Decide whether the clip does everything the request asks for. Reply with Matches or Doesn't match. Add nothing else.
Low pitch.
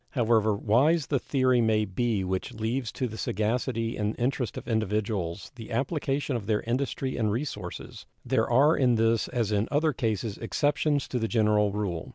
Matches